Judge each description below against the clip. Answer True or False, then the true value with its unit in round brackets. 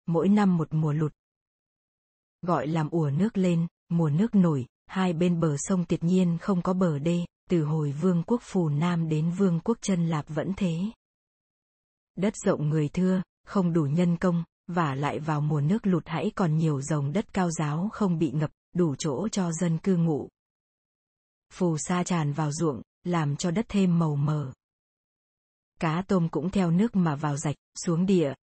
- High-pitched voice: False (170 Hz)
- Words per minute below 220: True (185 wpm)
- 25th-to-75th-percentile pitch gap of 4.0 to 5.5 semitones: False (3.2 semitones)